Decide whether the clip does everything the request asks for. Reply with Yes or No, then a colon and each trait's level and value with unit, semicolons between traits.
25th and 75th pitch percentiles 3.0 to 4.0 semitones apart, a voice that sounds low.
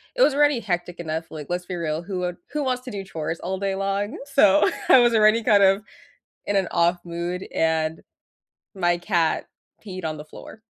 No: average, 3.3 semitones; medium, 185 Hz